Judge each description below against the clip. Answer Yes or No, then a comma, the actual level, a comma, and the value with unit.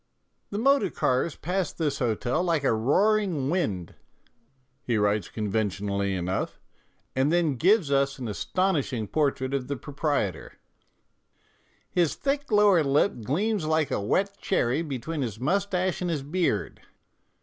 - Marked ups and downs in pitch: Yes, wide, 7.6 semitones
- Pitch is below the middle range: No, medium, 145 Hz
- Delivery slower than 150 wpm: Yes, average, 140 wpm